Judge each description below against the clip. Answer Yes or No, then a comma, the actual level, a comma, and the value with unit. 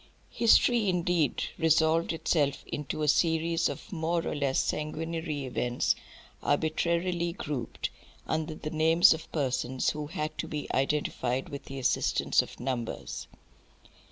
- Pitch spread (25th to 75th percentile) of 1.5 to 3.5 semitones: Yes, average, 2.8 semitones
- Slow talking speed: Yes, slow, 130 wpm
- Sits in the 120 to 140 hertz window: No, medium, 155 Hz